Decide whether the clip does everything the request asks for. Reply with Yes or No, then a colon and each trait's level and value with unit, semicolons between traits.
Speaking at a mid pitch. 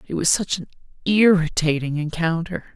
Yes: medium, 170 Hz